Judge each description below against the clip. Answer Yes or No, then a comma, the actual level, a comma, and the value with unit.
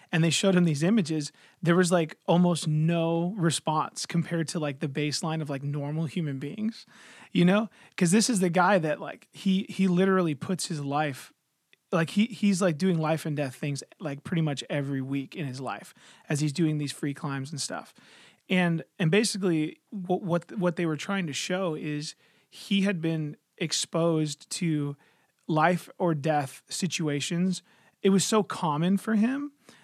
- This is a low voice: No, medium, 170 Hz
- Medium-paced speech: Yes, average, 180 wpm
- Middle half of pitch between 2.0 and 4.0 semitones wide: Yes, average, 3.7 semitones